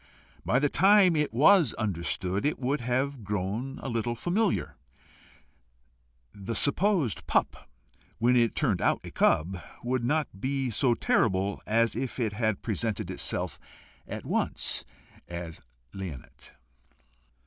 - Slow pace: Yes, slow, 125 wpm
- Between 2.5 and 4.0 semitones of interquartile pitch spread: No, wide, 5.5 semitones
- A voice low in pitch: Yes, low, 120 Hz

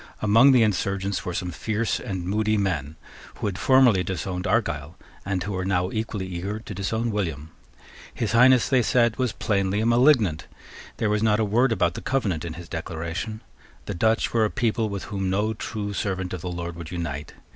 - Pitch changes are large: No, average, 3.8 semitones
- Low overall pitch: Yes, low, 100 Hz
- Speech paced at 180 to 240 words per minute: Yes, average, 195 wpm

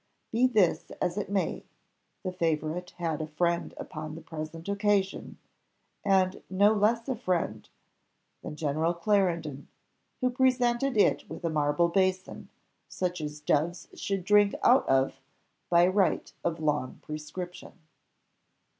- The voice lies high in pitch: No, medium, 180 Hz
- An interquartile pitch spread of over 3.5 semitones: Yes, average, 4.4 semitones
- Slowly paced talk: Yes, slow, 130 wpm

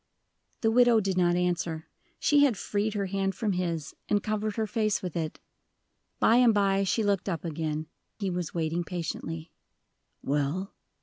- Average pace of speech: Yes, average, 165 wpm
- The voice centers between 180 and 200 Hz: Yes, high, 190 Hz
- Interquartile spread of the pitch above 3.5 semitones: Yes, average, 4.2 semitones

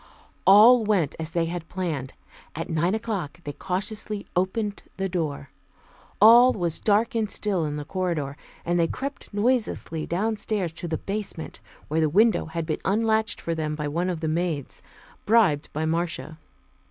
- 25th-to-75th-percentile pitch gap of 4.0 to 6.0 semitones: Yes, average, 4.9 semitones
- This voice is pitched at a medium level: Yes, medium, 175 Hz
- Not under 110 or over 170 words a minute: Yes, average, 165 wpm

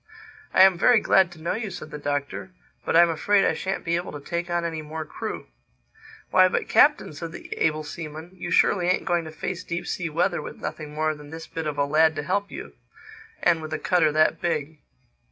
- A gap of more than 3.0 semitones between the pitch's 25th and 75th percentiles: No, average, 2.7 semitones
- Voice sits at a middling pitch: Yes, medium, 165 Hz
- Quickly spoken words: Yes, fast, 220 wpm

